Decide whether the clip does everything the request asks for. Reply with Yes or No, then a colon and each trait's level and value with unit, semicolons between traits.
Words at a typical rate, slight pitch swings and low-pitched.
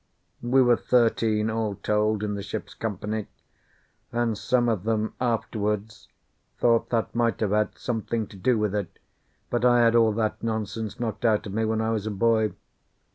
Yes: average, 180 wpm; narrow, 1.7 semitones; low, 110 Hz